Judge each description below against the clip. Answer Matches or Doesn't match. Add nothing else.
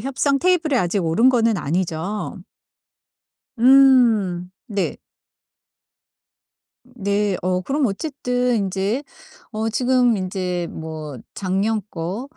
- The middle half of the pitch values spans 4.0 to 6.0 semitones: Matches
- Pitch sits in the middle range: Doesn't match